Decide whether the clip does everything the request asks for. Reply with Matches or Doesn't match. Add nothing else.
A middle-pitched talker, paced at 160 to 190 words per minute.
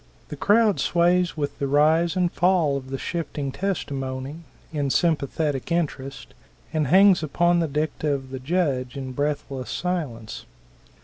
Doesn't match